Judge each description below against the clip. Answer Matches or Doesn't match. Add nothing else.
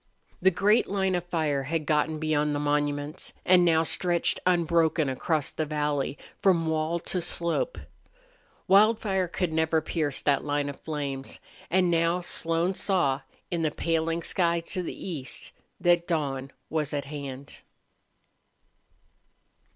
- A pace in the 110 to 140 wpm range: Matches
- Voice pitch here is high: Doesn't match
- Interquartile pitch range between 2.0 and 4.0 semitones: Matches